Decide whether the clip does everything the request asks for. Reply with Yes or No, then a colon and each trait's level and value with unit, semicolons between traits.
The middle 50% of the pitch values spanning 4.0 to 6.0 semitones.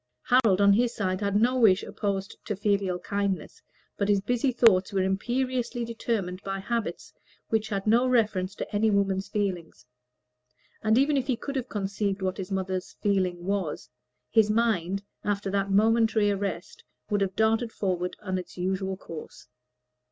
No: average, 2.8 semitones